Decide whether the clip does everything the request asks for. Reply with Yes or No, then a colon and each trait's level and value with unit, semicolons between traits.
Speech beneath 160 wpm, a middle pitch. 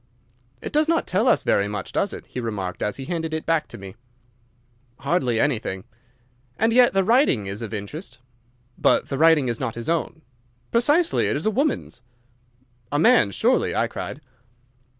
No: average, 175 wpm; medium, 150 Hz